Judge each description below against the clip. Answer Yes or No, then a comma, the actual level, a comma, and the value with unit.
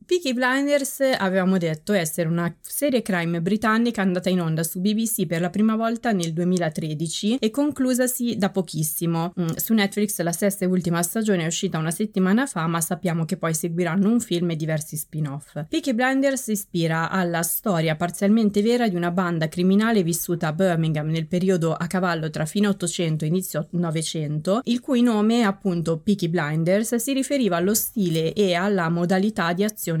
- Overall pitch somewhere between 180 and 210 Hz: Yes, medium, 185 Hz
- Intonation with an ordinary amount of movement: Yes, average, 4.2 semitones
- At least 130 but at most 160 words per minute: No, fast, 170 wpm